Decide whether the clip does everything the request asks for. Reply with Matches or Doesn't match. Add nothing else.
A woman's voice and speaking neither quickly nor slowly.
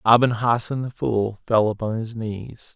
Doesn't match